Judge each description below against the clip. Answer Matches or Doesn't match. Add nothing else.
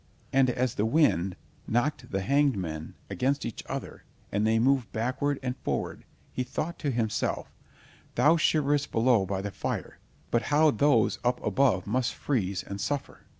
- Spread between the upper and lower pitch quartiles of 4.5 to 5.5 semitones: Matches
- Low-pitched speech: Matches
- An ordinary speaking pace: Matches